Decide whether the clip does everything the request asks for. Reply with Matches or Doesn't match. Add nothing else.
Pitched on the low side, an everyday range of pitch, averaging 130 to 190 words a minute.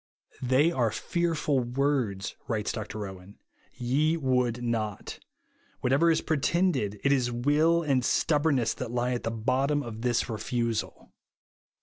Matches